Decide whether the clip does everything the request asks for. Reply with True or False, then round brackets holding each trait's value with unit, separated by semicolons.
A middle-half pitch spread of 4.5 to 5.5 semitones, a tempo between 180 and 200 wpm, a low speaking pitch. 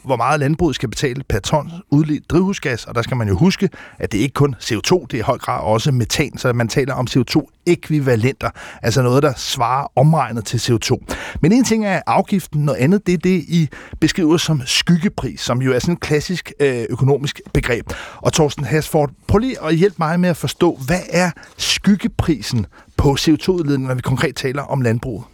False (5.1 semitones; 195 wpm; 145 Hz)